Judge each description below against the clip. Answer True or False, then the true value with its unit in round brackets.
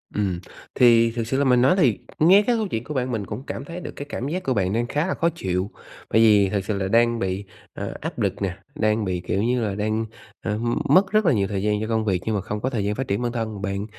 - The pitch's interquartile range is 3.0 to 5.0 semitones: True (4.4 semitones)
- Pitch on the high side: False (110 Hz)